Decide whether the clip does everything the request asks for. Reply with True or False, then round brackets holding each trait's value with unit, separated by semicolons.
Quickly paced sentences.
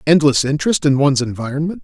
False (165 wpm)